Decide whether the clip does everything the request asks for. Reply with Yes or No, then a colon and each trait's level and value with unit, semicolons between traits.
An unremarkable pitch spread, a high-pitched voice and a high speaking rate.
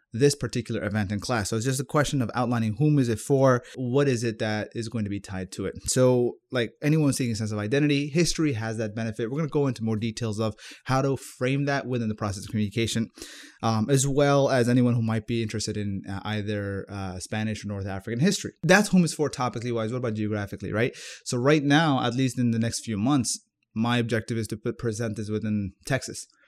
No: average, 3.7 semitones; low, 115 Hz; fast, 235 wpm